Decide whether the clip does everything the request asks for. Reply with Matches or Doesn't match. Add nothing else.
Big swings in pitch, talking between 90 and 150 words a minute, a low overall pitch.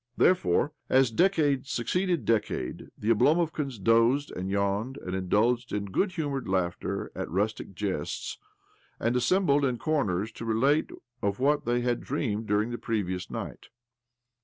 Matches